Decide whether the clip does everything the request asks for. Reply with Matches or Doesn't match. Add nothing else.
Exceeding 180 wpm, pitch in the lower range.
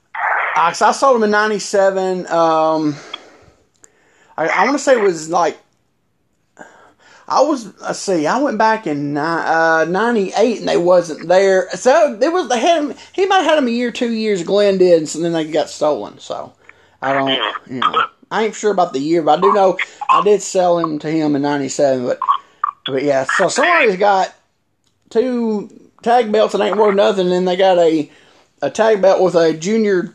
Doesn't match